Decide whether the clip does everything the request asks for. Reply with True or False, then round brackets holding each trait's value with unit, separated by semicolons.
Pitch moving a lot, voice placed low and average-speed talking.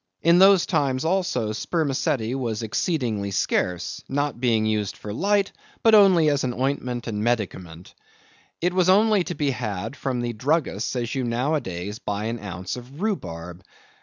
True (6.9 semitones; 125 Hz; 160 wpm)